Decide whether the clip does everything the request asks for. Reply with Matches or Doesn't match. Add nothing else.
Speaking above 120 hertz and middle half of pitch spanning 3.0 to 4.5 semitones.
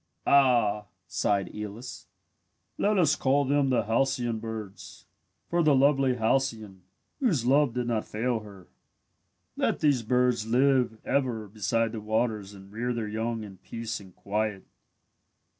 Doesn't match